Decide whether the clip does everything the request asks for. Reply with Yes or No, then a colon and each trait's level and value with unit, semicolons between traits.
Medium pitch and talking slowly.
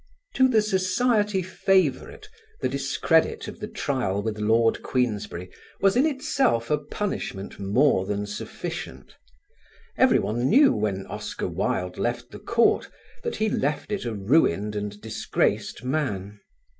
No: low, 130 Hz; slow, 130 wpm